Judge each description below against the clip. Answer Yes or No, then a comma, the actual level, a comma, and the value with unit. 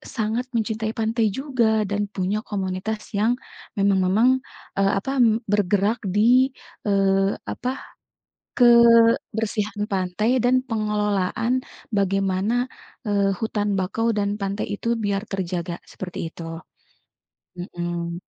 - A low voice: No, high, 200 Hz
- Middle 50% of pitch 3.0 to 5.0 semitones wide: No, narrow, 2.4 semitones